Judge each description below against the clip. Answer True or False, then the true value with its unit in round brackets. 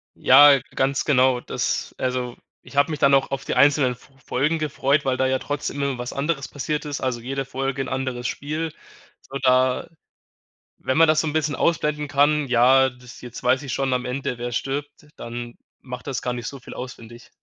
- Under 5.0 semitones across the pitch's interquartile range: True (2.4 semitones)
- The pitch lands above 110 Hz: True (135 Hz)